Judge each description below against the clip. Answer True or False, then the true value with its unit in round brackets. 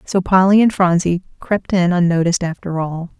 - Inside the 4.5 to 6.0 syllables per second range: True (5.2 syllables/s)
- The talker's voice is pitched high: False (180 Hz)